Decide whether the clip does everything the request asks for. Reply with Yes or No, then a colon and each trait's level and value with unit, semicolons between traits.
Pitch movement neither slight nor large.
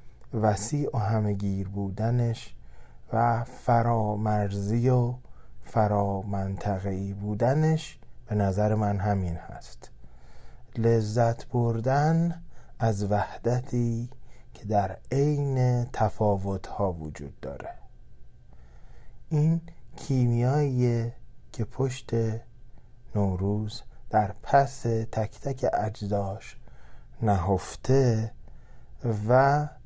Yes: average, 3.3 semitones